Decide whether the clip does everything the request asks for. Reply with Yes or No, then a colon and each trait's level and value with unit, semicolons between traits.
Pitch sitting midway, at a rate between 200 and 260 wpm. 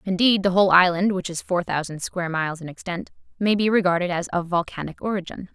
Yes: medium, 180 Hz; fast, 205 wpm